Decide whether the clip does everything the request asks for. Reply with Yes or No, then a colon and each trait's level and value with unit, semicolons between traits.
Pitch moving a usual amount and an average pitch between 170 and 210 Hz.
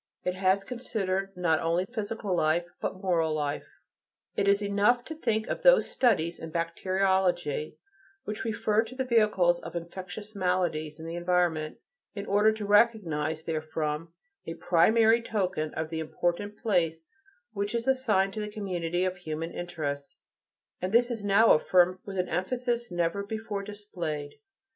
Yes: average, 4.1 semitones; medium, 185 Hz